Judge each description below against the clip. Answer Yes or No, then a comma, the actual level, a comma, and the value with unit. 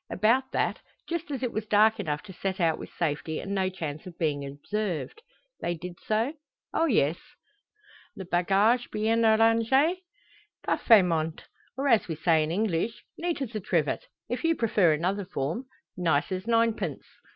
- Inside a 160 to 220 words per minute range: Yes, average, 165 wpm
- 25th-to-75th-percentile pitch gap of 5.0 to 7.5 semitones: Yes, wide, 5.5 semitones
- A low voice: No, high, 200 Hz